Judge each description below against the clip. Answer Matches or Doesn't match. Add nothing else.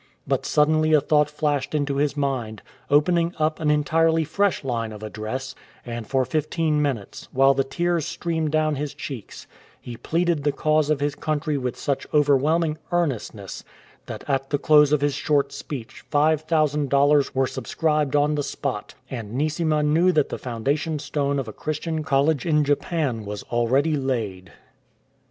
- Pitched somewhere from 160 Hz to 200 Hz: Doesn't match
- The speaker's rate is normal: Matches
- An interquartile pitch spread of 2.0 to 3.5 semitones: Matches